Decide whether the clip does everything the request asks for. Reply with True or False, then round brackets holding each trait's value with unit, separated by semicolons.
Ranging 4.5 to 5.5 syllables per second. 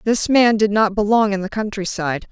True (5.0 syllables/s)